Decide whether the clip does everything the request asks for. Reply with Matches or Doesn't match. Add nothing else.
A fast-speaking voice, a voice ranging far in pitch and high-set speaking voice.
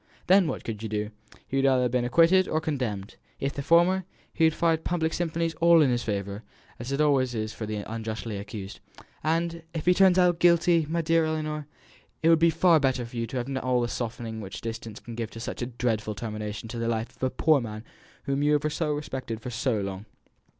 Doesn't match